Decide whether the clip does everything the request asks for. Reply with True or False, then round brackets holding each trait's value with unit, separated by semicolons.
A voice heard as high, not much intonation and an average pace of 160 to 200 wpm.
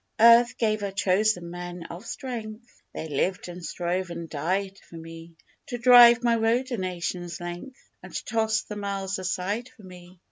False (195 Hz; 4.3 semitones; 170 wpm)